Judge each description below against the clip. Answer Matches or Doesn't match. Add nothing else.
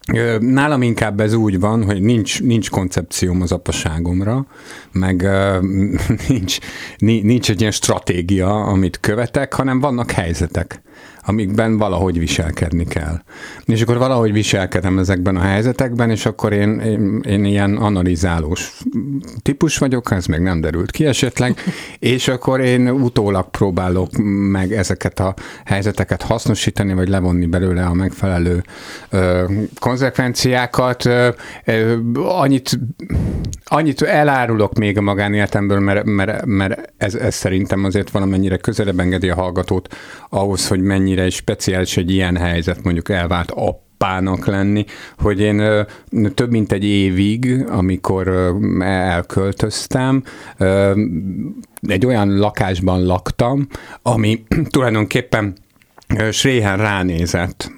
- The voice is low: Matches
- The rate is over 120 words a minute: Doesn't match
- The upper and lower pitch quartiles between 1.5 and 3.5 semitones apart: Doesn't match